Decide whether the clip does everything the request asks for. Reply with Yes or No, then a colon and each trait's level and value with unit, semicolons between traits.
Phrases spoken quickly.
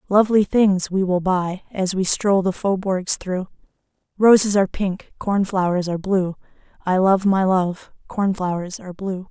No: average, 170 wpm